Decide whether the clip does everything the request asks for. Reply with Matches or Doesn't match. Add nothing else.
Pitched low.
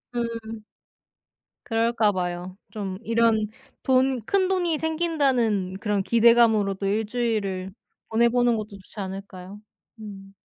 Doesn't match